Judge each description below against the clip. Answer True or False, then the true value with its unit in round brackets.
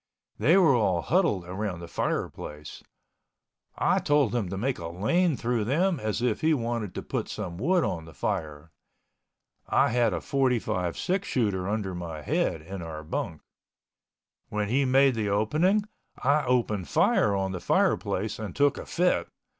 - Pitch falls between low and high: False (110 Hz)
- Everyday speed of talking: True (165 wpm)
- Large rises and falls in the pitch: True (7.0 semitones)